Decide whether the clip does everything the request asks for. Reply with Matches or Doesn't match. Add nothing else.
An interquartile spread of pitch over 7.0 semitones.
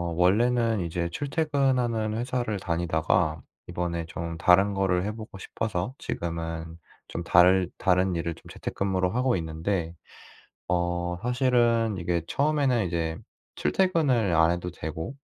Doesn't match